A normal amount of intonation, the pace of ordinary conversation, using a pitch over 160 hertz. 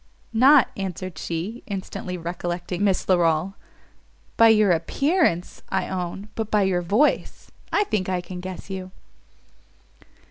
No: average, 3.2 semitones; slow, 130 wpm; high, 190 Hz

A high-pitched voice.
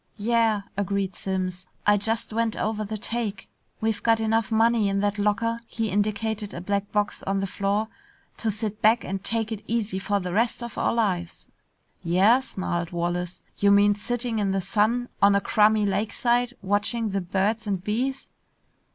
Yes: high, 210 Hz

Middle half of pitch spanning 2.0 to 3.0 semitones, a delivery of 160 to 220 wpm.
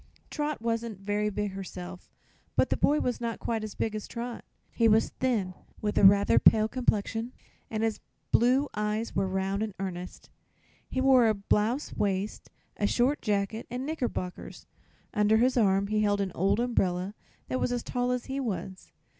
No: average, 3.5 semitones; average, 175 wpm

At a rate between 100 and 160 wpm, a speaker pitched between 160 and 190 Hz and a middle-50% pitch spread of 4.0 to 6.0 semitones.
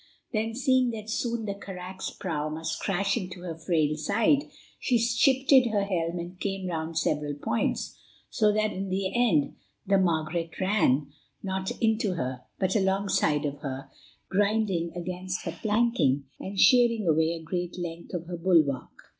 Yes: average, 155 wpm; medium, 185 Hz; average, 4.6 semitones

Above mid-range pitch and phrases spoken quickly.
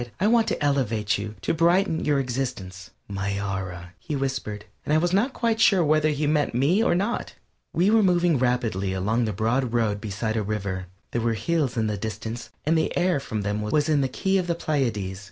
No: low, 125 Hz; fast, 210 wpm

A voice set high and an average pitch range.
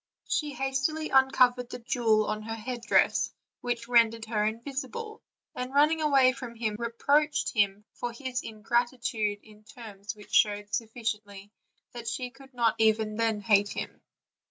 Yes: high, 235 Hz; average, 3.2 semitones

